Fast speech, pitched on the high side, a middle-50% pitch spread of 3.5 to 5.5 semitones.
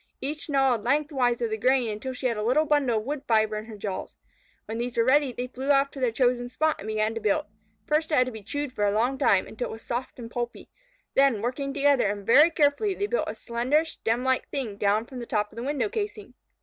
Yes: fast, 255 wpm; very high, 250 Hz; average, 4.2 semitones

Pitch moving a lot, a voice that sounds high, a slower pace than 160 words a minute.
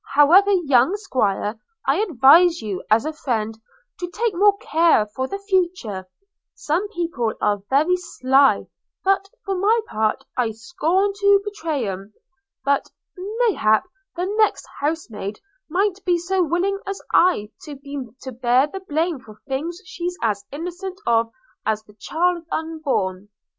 Yes: wide, 8.0 semitones; very high, 315 Hz; average, 150 wpm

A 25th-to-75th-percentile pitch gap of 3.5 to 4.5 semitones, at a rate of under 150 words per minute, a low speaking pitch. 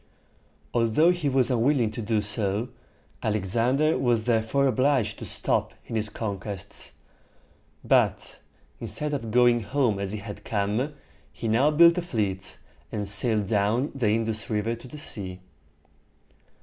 Yes: average, 3.8 semitones; average, 140 wpm; low, 115 Hz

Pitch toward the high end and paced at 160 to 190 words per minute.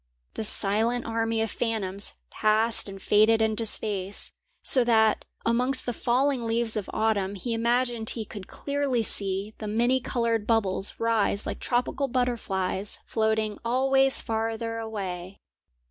No: high, 225 Hz; slow, 135 wpm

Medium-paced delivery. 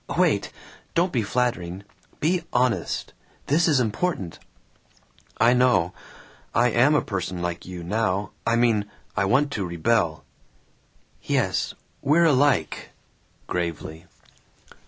No: slow, 115 wpm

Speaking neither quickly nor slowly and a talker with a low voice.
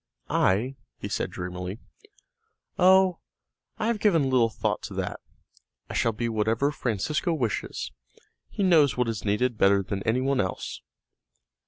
Yes: average, 145 wpm; low, 120 Hz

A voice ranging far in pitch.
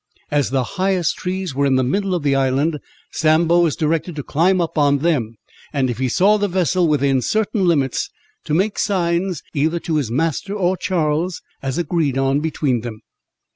No: average, 4.8 semitones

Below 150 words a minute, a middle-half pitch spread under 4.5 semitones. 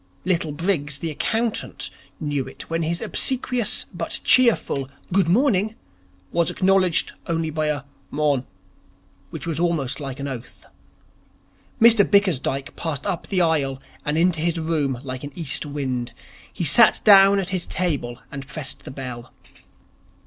No: average, 140 wpm; average, 4.8 semitones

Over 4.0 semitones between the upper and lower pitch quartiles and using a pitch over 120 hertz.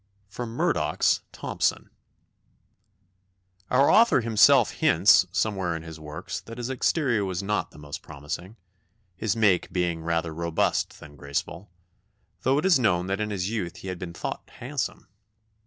No: average, 5.3 semitones; very low, 95 Hz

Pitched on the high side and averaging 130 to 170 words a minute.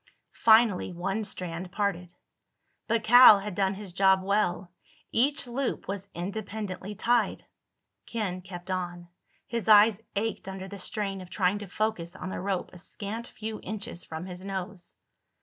Yes: high, 195 Hz; average, 150 wpm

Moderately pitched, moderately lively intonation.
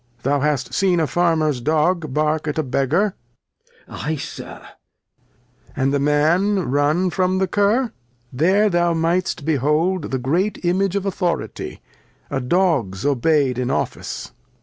Yes: medium, 160 Hz; average, 4.4 semitones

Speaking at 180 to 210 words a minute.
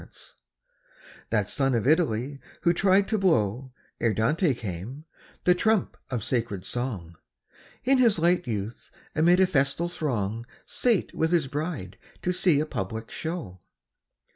No: average, 140 wpm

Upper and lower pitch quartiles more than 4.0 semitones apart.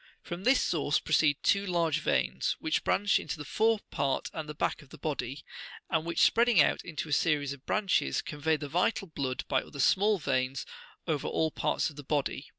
No: average, 3.7 semitones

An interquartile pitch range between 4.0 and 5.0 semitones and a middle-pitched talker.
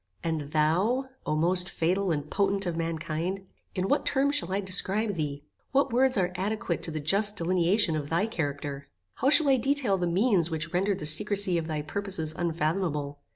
Yes: average, 4.3 semitones; medium, 180 Hz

